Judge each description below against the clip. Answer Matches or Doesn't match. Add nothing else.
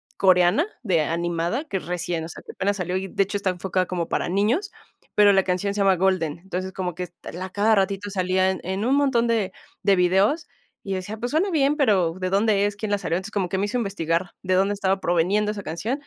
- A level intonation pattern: Matches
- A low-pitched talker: Doesn't match